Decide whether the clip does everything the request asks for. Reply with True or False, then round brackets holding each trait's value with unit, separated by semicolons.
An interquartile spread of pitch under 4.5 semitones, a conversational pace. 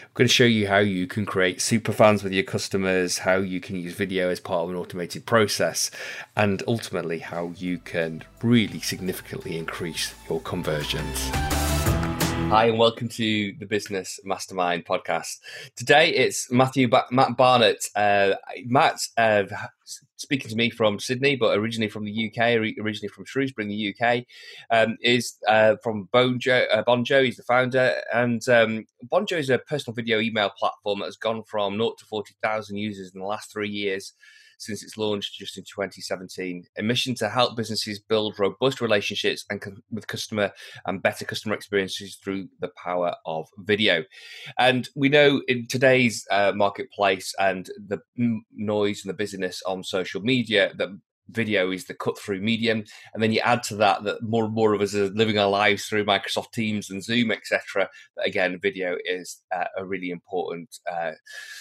True (3.5 semitones; 175 wpm)